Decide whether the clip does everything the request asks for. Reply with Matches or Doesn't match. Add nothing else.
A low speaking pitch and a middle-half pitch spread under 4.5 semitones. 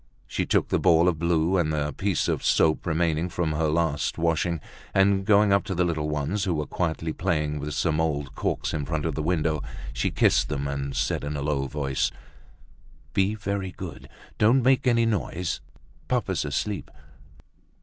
Matches